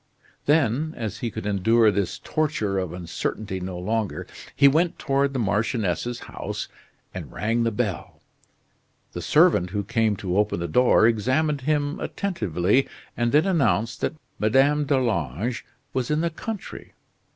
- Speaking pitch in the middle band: No, low, 115 Hz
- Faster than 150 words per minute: No, average, 145 wpm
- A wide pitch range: Yes, wide, 5.8 semitones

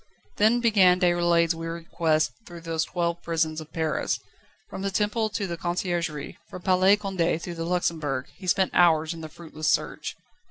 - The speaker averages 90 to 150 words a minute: No, average, 170 wpm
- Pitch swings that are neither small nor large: No, narrow, 2.2 semitones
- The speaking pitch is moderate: Yes, medium, 170 Hz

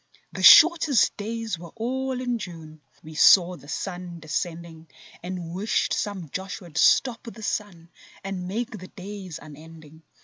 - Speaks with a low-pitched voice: No, medium, 185 Hz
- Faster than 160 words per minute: No, average, 140 wpm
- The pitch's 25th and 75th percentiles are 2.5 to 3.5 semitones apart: No, average, 5.0 semitones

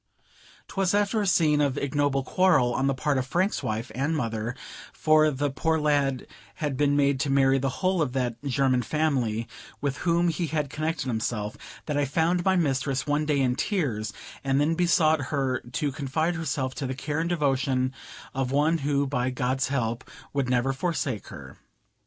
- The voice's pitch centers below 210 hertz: Yes, medium, 140 Hz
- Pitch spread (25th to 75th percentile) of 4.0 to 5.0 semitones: No, average, 3.2 semitones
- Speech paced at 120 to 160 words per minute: No, average, 180 wpm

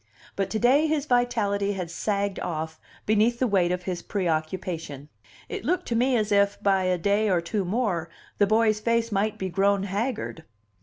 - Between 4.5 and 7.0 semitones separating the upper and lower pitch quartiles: No, average, 3.8 semitones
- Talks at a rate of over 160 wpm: Yes, average, 185 wpm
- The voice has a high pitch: Yes, high, 200 Hz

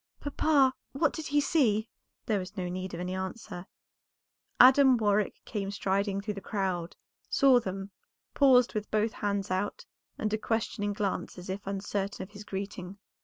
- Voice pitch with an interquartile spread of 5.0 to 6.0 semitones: No, average, 3.1 semitones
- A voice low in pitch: No, high, 205 Hz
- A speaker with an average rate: Yes, average, 165 wpm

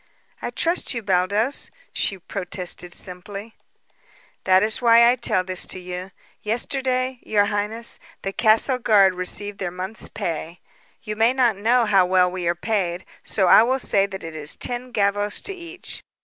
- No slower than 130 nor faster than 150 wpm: No, average, 165 wpm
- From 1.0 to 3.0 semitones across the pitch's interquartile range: No, average, 4.1 semitones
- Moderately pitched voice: No, high, 205 Hz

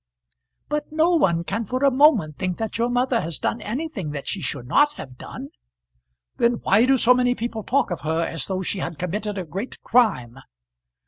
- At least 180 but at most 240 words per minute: Yes, average, 200 wpm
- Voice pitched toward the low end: No, high, 215 Hz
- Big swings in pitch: Yes, wide, 6.8 semitones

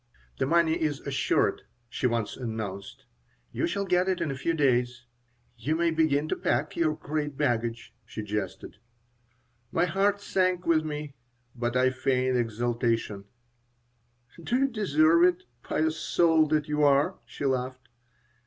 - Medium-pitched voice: Yes, medium, 145 Hz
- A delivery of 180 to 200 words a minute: No, average, 145 wpm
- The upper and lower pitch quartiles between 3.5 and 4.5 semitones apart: No, average, 5.3 semitones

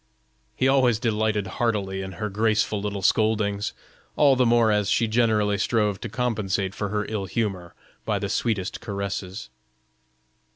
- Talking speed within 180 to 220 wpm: No, average, 150 wpm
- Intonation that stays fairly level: Yes, narrow, 2.3 semitones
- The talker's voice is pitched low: Yes, low, 105 Hz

